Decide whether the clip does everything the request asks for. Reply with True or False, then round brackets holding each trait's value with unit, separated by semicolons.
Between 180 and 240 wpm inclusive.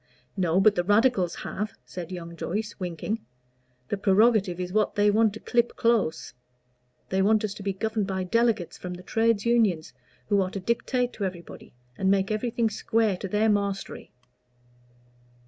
False (165 wpm)